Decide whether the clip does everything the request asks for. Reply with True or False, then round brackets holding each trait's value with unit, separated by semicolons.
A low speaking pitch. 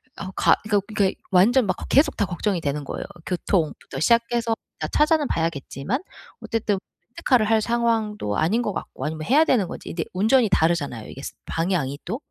False (200 Hz)